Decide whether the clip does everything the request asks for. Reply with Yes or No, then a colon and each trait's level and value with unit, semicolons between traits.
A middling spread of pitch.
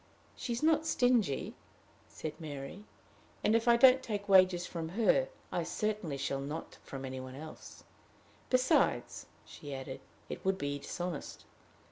No: wide, 8.4 semitones